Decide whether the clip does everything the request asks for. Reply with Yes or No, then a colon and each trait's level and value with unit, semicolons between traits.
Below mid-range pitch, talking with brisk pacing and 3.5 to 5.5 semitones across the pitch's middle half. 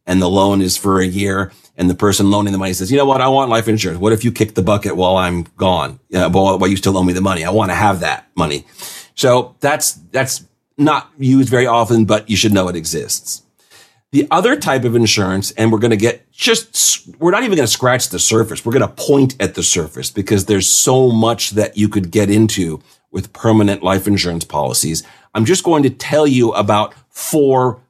Yes: low, 105 Hz; fast, 225 wpm; average, 4.8 semitones